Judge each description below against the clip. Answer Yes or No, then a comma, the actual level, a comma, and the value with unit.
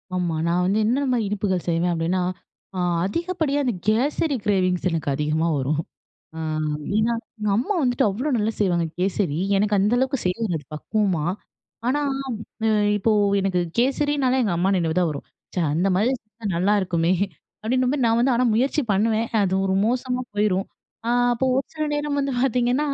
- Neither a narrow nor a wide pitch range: No, wide, 5.7 semitones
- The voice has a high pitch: Yes, high, 215 Hz